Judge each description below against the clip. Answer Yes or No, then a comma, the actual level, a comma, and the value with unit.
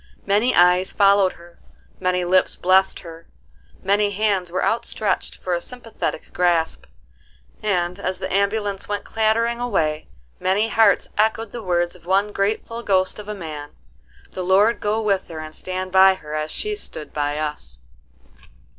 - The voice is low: No, high, 190 Hz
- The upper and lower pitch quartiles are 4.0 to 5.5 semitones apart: No, average, 3.2 semitones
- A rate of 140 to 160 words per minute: Yes, average, 155 wpm